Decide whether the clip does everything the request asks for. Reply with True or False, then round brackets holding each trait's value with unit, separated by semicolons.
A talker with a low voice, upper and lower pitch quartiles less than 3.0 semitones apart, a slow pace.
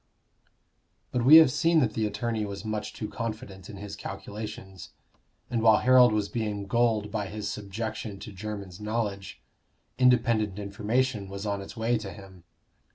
False (105 Hz; 2.4 semitones; 160 wpm)